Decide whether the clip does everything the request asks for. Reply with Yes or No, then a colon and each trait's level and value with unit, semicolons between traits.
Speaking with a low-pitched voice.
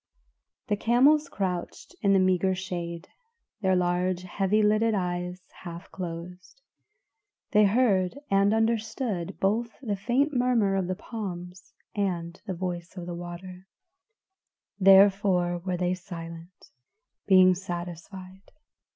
No: medium, 185 Hz